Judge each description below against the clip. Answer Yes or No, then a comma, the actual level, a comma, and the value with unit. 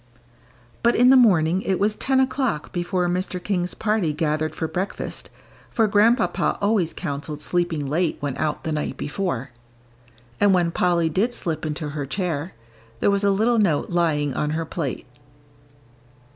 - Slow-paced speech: No, average, 160 wpm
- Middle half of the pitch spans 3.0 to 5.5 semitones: Yes, average, 4.7 semitones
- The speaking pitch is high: No, medium, 175 Hz